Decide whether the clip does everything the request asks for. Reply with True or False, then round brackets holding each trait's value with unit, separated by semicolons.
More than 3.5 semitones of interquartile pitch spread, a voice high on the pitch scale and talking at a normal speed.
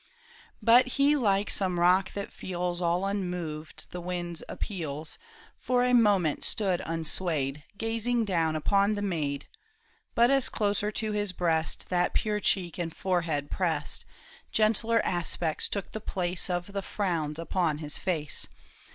False (3.9 semitones; 180 Hz; 145 wpm)